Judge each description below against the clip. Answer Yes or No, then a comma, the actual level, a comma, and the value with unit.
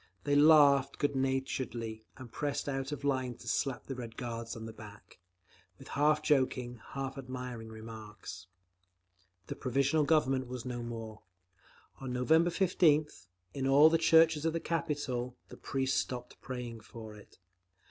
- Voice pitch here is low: Yes, low, 130 Hz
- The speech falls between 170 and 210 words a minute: No, average, 150 wpm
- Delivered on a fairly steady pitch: No, average, 3.7 semitones